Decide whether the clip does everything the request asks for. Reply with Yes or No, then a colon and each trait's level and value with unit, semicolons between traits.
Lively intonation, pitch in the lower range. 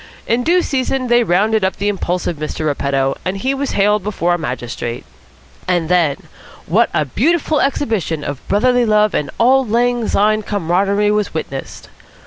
No: wide, 6.5 semitones; high, 205 Hz